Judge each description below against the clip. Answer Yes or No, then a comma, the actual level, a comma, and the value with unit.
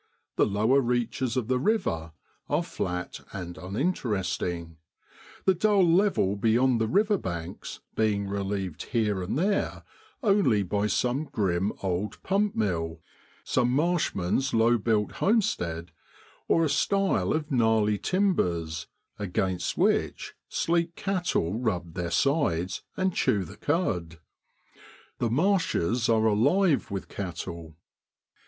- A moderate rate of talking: No, slow, 120 wpm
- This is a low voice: Yes, low, 110 Hz